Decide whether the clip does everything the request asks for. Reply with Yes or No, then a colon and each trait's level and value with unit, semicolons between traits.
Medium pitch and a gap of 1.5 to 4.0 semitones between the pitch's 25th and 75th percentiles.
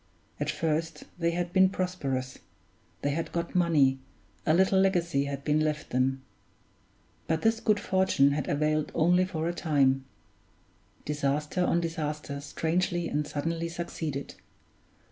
Yes: medium, 160 Hz; average, 3.4 semitones